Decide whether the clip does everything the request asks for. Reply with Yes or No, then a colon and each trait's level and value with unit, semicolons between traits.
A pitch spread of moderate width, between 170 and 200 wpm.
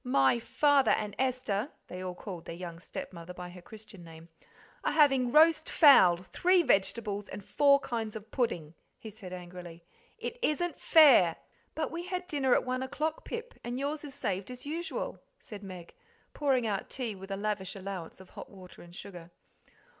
No: wide, 7.6 semitones; average, 175 wpm